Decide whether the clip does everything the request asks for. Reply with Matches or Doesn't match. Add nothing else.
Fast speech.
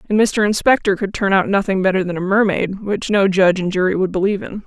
Matches